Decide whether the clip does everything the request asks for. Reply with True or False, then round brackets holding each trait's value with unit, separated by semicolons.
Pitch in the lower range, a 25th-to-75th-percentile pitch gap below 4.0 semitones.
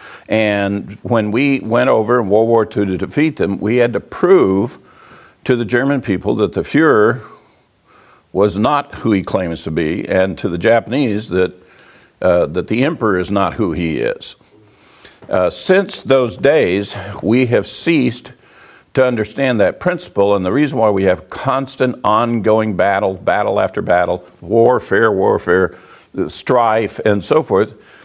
False (110 Hz; 4.3 semitones)